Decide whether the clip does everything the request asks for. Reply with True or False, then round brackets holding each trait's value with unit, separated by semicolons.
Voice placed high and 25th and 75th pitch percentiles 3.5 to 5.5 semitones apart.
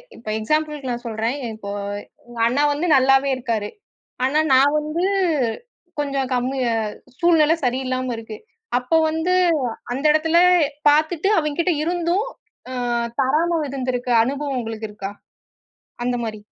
True (265 Hz; 4.0 semitones)